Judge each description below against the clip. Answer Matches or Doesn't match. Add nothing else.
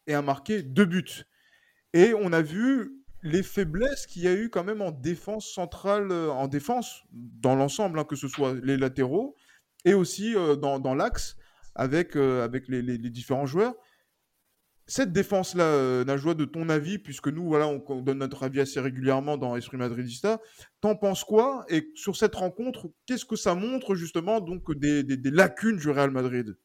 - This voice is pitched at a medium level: Matches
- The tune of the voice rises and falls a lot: Matches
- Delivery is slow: Doesn't match